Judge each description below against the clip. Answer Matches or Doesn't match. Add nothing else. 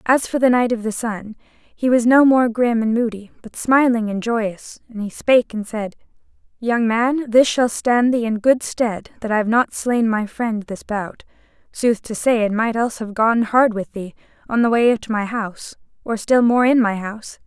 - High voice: Matches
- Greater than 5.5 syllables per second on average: Doesn't match